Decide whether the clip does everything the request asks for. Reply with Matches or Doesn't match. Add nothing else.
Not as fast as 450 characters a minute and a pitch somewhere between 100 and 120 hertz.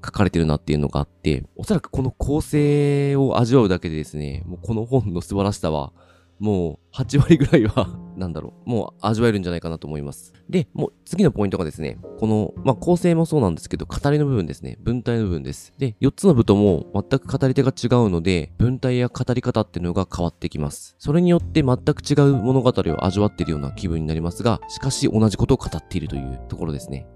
Doesn't match